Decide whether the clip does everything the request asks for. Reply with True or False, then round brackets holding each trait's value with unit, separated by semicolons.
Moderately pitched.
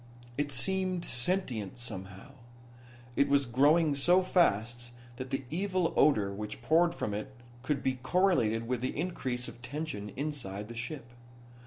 False (130 Hz)